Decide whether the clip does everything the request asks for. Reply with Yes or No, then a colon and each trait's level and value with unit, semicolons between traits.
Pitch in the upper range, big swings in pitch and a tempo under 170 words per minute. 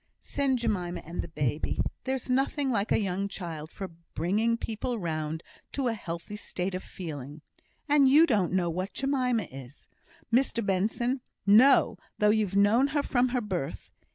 Yes: high, 205 Hz; wide, 6.3 semitones; average, 160 wpm